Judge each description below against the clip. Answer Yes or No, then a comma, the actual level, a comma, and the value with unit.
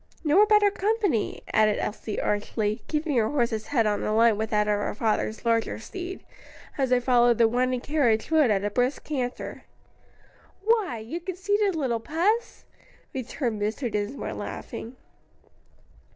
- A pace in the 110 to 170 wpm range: Yes, average, 150 wpm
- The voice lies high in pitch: Yes, high, 245 Hz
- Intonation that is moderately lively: No, wide, 6.5 semitones